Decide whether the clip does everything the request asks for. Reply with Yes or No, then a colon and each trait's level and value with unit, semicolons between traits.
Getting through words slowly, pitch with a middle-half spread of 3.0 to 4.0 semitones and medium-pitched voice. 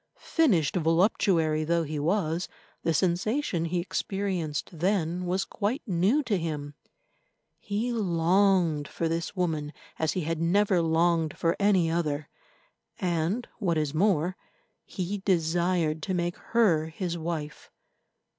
Yes: slow, 125 wpm; average, 3.3 semitones; medium, 170 Hz